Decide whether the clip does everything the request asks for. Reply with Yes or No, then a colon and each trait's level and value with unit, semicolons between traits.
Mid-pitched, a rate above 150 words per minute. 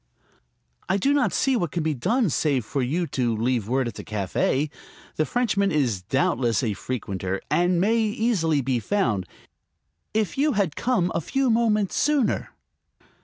Yes: medium, 165 Hz; average, 165 wpm